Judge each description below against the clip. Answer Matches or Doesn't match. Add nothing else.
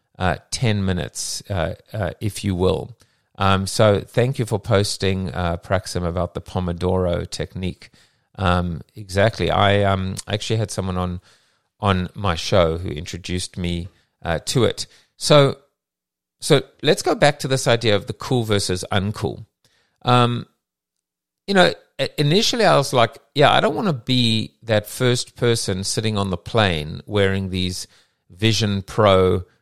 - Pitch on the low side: Matches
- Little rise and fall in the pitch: Doesn't match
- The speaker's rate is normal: Matches